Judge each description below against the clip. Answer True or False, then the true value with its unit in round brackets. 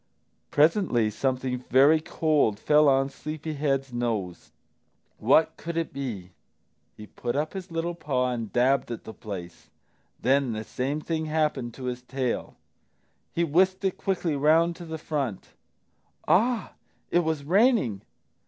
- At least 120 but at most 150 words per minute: True (145 wpm)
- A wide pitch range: False (4.6 semitones)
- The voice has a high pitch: False (140 Hz)